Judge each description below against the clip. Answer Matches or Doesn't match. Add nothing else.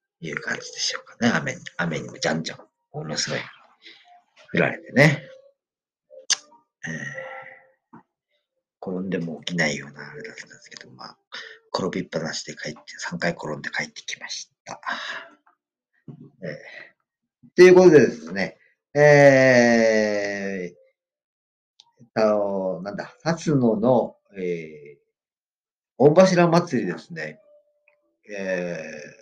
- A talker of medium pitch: Matches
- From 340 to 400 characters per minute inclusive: Doesn't match